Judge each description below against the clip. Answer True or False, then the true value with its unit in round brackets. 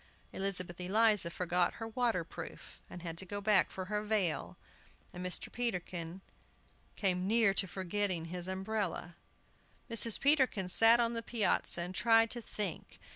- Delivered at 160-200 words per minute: False (145 wpm)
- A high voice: True (195 Hz)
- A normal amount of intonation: True (3.9 semitones)